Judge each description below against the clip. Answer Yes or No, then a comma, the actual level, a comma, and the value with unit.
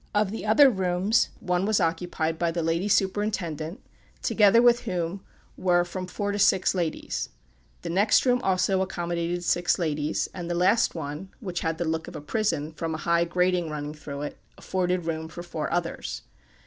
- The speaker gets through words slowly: No, average, 180 wpm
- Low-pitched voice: No, medium, 175 Hz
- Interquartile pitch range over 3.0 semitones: No, average, 2.7 semitones